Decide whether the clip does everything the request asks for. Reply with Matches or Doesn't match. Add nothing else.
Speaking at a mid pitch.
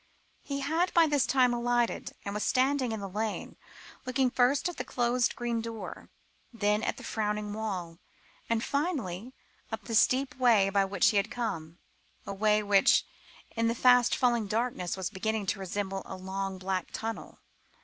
Doesn't match